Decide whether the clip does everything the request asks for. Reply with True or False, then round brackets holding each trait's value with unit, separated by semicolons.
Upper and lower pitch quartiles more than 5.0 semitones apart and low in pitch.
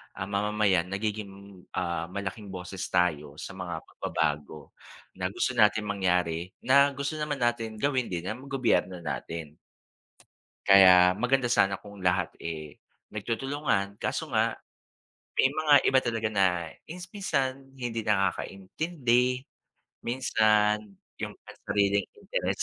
True (5.5 semitones; 105 Hz)